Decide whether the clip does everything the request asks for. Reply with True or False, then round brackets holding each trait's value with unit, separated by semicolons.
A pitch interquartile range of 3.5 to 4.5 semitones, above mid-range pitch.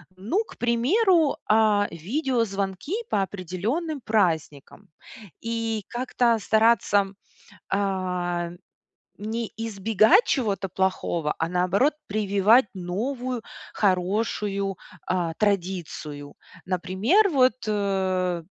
True (4.0 semitones; 205 Hz)